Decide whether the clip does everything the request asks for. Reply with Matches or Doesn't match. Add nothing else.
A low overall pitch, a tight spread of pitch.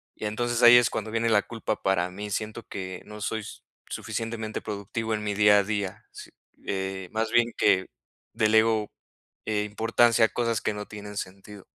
Matches